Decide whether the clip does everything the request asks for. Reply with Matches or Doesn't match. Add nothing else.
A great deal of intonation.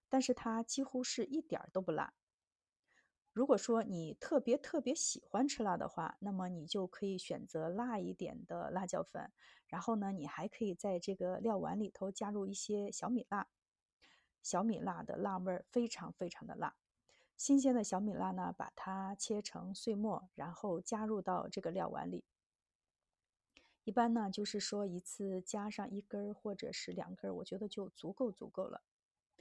Doesn't match